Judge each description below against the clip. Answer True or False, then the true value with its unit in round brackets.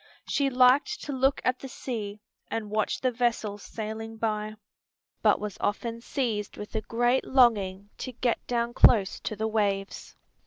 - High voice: True (225 Hz)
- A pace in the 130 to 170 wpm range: True (160 wpm)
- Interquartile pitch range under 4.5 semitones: True (3.0 semitones)